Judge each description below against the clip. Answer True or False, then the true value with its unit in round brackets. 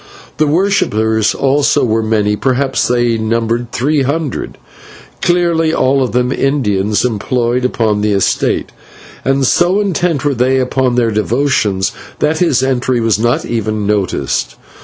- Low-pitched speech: True (125 Hz)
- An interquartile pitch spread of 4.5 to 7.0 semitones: False (4.1 semitones)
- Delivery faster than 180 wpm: False (140 wpm)